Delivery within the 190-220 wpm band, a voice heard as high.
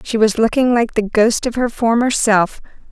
Yes: fast, 205 wpm; high, 225 Hz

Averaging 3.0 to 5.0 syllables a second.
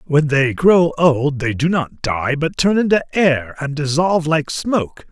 Yes: 4.2 syllables/s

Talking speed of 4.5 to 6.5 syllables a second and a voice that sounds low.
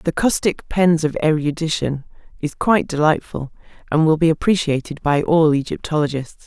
No: 5.1 syllables/s; medium, 155 Hz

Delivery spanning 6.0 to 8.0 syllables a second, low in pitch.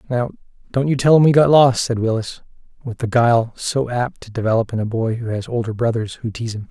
Yes: 6.1 syllables/s; low, 120 Hz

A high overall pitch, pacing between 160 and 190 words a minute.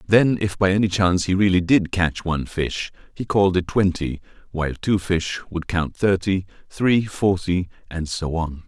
No: very low, 90 Hz; average, 180 wpm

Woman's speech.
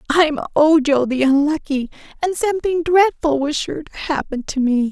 Yes: female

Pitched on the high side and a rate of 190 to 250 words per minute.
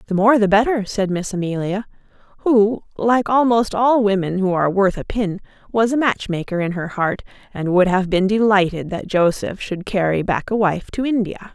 Yes: high, 200 Hz; average, 195 wpm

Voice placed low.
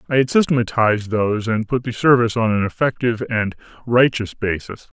Yes: low, 115 Hz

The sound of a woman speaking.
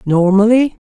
No: male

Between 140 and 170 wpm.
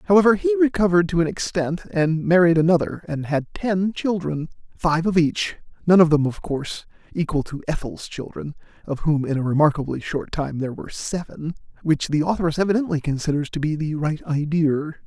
No: average, 180 wpm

